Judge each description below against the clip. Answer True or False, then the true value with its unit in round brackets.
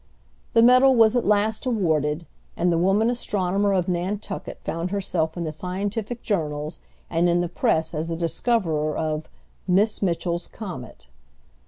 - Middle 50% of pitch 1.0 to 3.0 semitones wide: False (4.3 semitones)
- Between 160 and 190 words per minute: False (150 wpm)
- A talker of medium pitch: True (180 Hz)